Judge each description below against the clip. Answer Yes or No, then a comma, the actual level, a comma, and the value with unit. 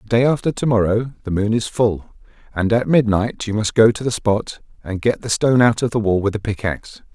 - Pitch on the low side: Yes, low, 110 Hz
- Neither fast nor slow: No, fast, 245 wpm